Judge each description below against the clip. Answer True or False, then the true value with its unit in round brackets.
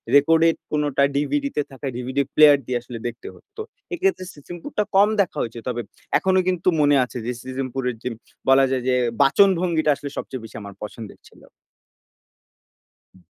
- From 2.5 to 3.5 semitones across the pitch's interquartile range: False (5.0 semitones)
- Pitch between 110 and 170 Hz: True (140 Hz)